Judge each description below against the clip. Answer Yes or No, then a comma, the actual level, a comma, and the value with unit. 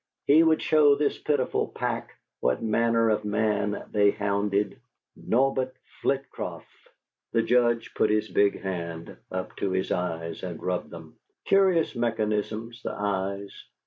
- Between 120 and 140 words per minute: Yes, slow, 135 wpm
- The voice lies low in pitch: Yes, low, 110 Hz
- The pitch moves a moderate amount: Yes, average, 3.8 semitones